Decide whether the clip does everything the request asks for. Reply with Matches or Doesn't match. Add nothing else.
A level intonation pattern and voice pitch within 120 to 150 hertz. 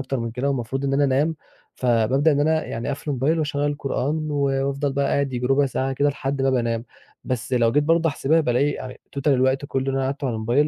Matches